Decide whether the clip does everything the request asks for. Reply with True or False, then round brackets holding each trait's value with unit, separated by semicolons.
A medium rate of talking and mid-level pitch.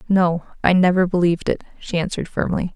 True (175 wpm; 175 Hz)